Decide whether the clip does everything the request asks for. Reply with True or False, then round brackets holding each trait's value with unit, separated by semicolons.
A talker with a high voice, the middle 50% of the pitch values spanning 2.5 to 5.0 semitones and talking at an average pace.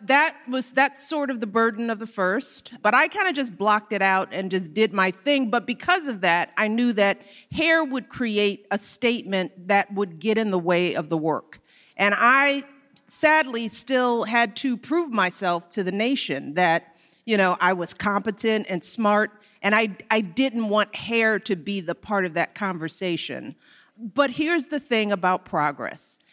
True (215 Hz; 4.7 semitones; 185 wpm)